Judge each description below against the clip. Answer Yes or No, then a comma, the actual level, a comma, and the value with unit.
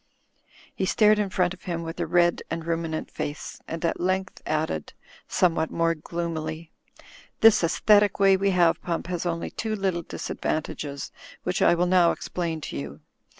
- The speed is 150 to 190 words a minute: Yes, average, 165 wpm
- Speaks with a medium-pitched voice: Yes, medium, 170 Hz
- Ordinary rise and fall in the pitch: No, narrow, 2.3 semitones